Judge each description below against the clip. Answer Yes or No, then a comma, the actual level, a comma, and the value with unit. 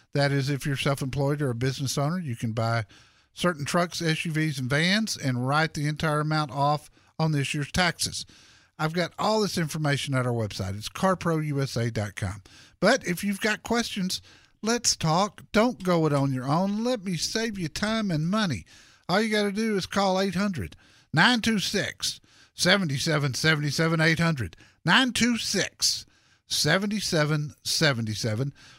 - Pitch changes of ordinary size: No, wide, 5.9 semitones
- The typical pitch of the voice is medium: Yes, medium, 155 Hz